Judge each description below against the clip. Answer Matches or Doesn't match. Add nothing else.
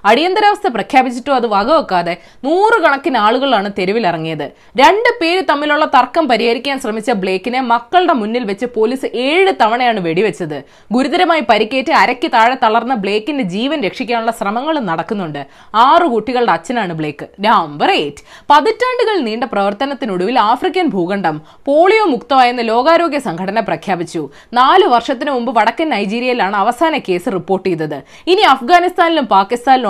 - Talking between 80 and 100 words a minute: Doesn't match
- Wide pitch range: Matches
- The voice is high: Matches